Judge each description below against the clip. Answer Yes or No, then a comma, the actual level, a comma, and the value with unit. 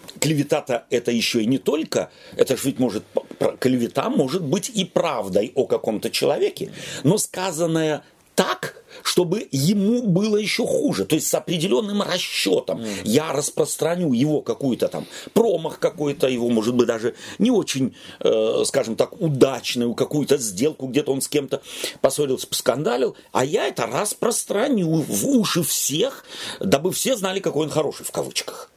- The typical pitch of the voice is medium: Yes, medium, 175 Hz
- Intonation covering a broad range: Yes, wide, 6.4 semitones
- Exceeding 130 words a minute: Yes, average, 145 wpm